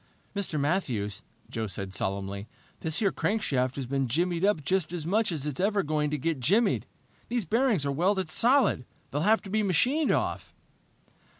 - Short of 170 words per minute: No, average, 175 wpm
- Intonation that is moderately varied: No, wide, 7.1 semitones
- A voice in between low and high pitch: Yes, medium, 165 Hz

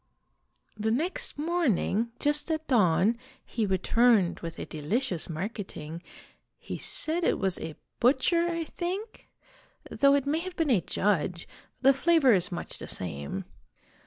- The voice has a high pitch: Yes, high, 235 Hz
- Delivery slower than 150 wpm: Yes, average, 140 wpm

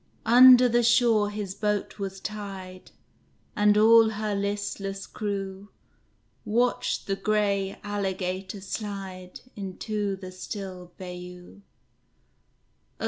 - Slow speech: Yes, slow, 95 wpm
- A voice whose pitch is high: Yes, high, 200 Hz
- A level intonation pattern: Yes, narrow, 1.9 semitones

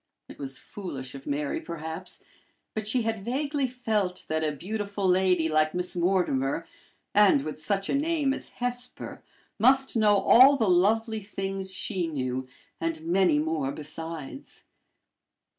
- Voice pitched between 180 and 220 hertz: Yes, medium, 185 Hz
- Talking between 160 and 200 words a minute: No, average, 140 wpm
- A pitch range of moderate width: No, wide, 5.8 semitones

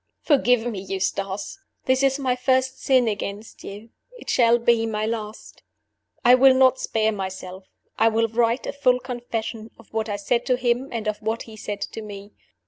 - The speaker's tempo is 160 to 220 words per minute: Yes, average, 185 wpm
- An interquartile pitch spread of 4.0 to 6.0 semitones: No, average, 2.9 semitones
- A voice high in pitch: Yes, high, 225 Hz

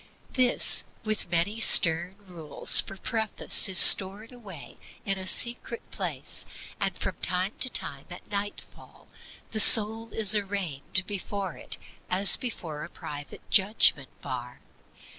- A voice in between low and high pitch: No, high, 195 Hz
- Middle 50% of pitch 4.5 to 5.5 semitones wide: No, average, 4.0 semitones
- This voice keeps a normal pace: No, slow, 130 wpm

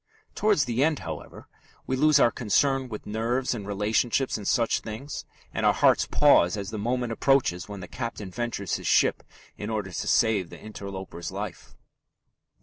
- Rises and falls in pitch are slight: No, average, 4.0 semitones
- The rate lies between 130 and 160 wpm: No, average, 170 wpm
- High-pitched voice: No, low, 110 Hz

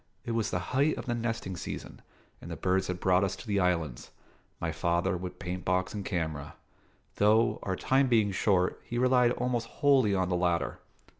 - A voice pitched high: No, very low, 95 Hz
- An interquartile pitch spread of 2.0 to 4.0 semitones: No, average, 4.5 semitones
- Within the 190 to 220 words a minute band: Yes, average, 195 wpm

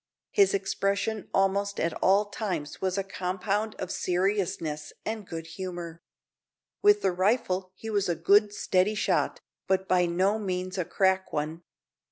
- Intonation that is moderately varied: No, narrow, 2.2 semitones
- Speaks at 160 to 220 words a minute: No, average, 150 wpm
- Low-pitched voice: No, high, 190 Hz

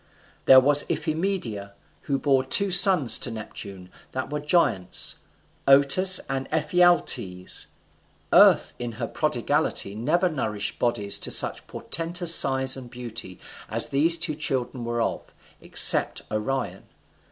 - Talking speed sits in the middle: No, slow, 125 wpm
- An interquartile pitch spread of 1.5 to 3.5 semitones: No, wide, 5.5 semitones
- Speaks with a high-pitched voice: No, low, 135 Hz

